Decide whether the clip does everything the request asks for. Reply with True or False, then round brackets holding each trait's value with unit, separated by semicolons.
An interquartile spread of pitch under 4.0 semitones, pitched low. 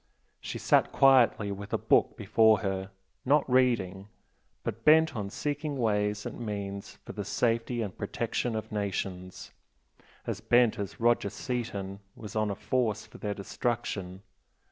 True (3.4 semitones; 110 Hz)